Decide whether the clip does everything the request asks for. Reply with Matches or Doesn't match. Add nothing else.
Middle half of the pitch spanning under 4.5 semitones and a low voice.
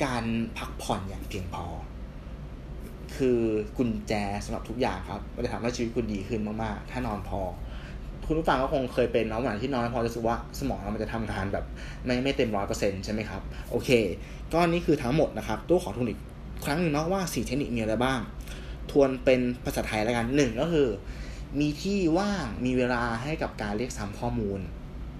Doesn't match